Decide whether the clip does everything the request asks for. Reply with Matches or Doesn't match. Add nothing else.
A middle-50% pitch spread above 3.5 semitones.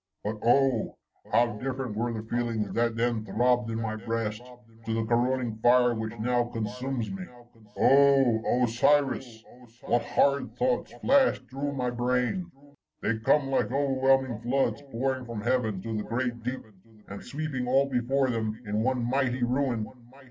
Doesn't match